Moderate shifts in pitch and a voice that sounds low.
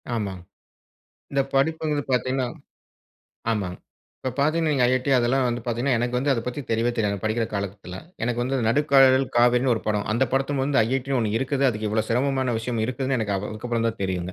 Yes: average, 3.3 semitones; low, 125 Hz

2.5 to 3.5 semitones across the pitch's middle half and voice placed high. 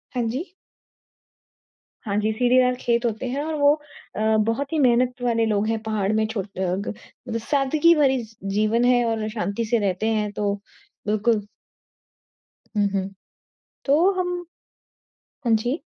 Yes: average, 3.2 semitones; high, 230 Hz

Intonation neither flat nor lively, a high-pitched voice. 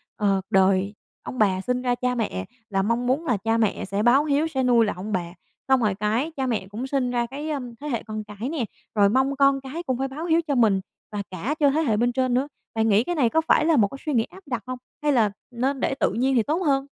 Yes: average, 4.3 semitones; high, 245 Hz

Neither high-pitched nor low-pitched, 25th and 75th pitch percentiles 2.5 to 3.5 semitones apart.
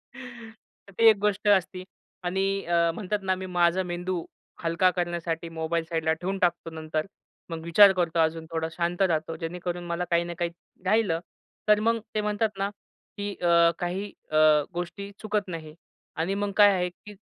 Yes: medium, 180 Hz; average, 3.0 semitones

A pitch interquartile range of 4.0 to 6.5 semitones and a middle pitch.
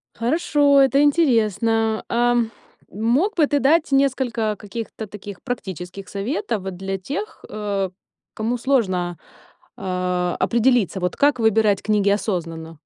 No: wide, 5.4 semitones; high, 220 Hz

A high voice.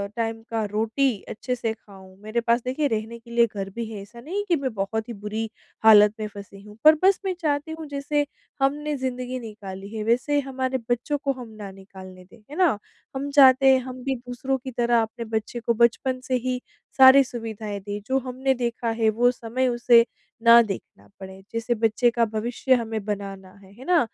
Yes: high, 235 Hz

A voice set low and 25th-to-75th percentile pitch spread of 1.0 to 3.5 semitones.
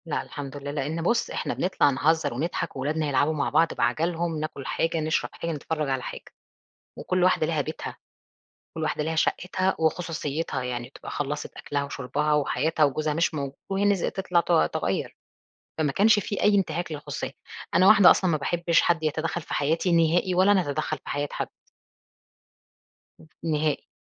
No: medium, 155 Hz; average, 3.0 semitones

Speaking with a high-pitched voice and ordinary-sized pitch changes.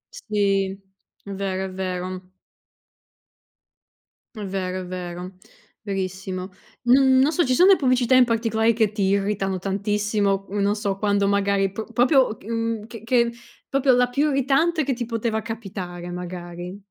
Yes: high, 205 Hz; average, 3.8 semitones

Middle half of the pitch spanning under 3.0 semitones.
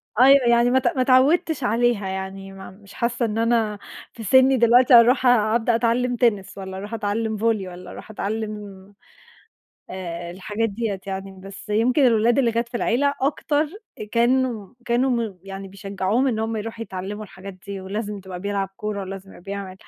No: average, 3.6 semitones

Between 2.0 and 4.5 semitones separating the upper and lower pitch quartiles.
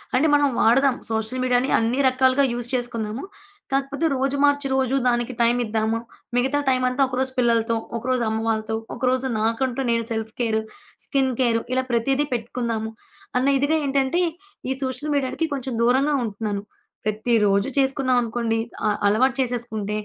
Yes: average, 2.7 semitones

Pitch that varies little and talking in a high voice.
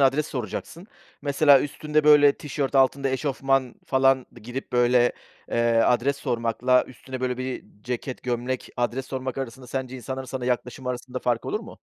No: narrow, 1.6 semitones; low, 130 Hz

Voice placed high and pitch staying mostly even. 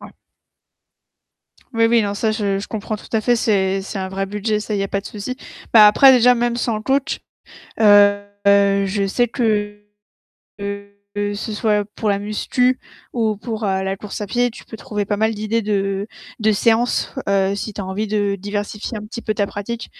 Yes: high, 210 Hz; narrow, 1.9 semitones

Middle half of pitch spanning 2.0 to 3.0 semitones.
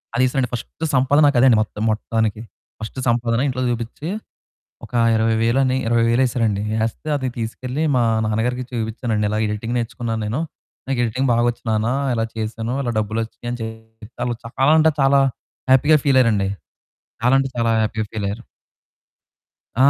Yes: narrow, 2.4 semitones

